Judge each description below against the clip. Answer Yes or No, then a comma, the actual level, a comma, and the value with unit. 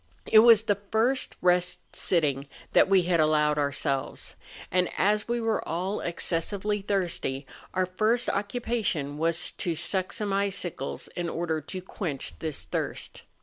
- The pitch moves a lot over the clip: No, average, 4.4 semitones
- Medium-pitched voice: Yes, medium, 180 Hz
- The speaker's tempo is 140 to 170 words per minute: Yes, average, 145 wpm